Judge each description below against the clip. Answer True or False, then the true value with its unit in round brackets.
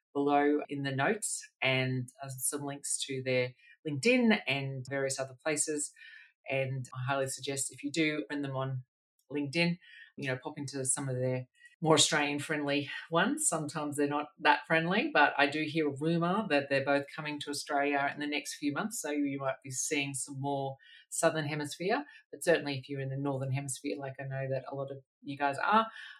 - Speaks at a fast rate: False (195 wpm)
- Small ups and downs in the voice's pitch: True (2.3 semitones)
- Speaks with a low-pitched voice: False (145 Hz)